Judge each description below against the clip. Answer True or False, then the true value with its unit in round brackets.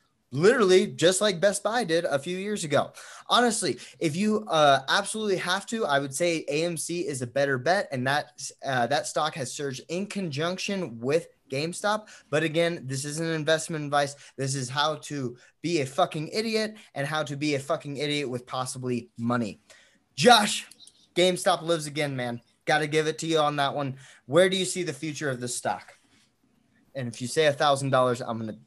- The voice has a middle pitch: True (150 Hz)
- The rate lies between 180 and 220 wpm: True (190 wpm)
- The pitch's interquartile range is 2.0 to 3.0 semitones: False (4.7 semitones)